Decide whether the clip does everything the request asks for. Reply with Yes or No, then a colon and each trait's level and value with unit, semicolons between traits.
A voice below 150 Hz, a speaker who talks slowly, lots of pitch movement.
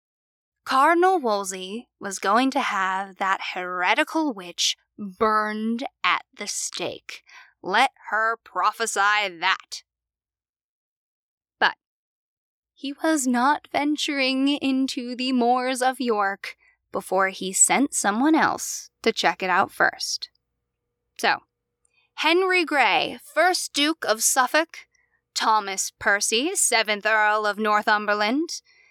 No: high, 245 Hz; slow, 105 wpm; wide, 6.5 semitones